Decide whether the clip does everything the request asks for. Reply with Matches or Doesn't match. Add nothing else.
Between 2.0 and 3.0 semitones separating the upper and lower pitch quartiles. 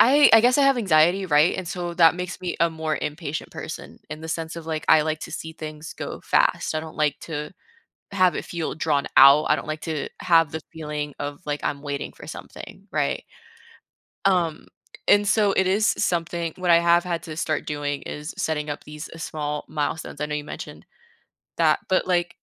Matches